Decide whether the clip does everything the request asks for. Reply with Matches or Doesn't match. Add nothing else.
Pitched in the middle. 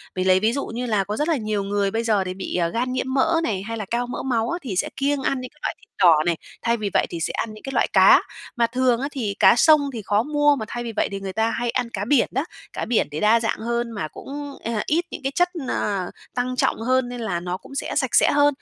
Doesn't match